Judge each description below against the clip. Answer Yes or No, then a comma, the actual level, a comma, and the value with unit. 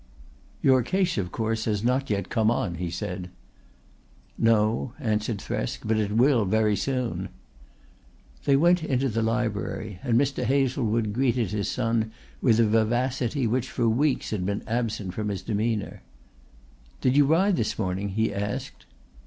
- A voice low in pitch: Yes, low, 115 Hz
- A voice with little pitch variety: No, average, 3.4 semitones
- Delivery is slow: No, average, 155 wpm